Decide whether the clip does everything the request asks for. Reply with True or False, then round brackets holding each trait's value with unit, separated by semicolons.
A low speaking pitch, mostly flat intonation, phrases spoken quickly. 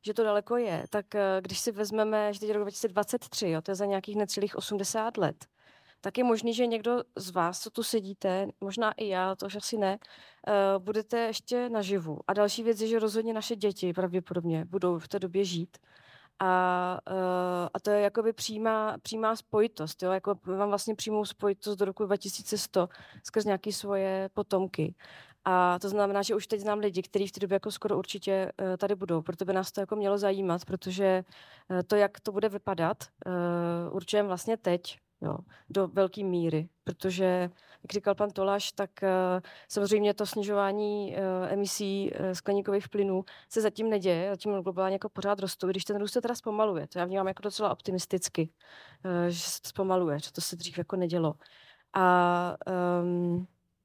False (195 Hz; 2.2 semitones; 175 wpm)